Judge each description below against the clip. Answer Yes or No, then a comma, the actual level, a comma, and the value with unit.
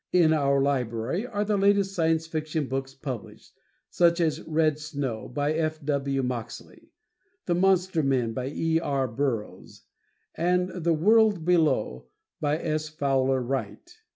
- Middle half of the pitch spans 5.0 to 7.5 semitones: No, average, 4.1 semitones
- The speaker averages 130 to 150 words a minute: Yes, average, 140 wpm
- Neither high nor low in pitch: Yes, medium, 155 Hz